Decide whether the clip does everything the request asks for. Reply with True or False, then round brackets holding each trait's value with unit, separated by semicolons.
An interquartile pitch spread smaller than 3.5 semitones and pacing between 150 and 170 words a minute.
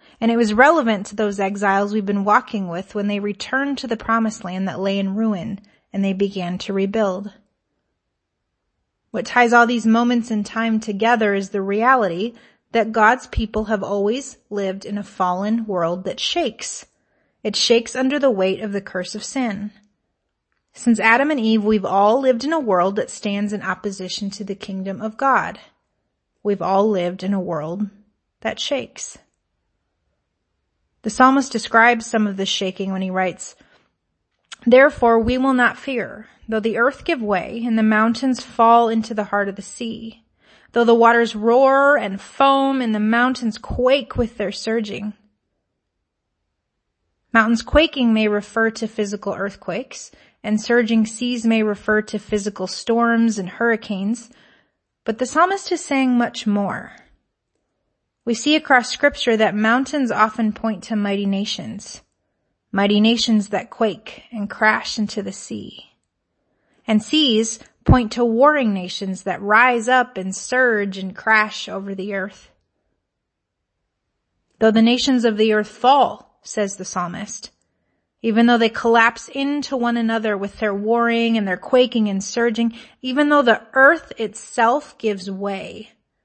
True (2.9 semitones; 155 wpm)